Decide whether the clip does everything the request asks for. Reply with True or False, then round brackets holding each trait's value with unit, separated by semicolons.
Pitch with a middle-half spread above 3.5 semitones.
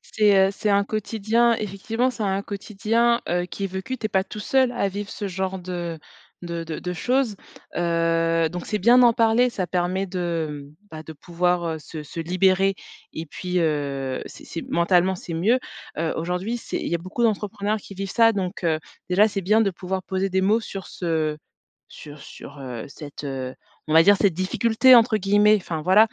True (4.1 semitones)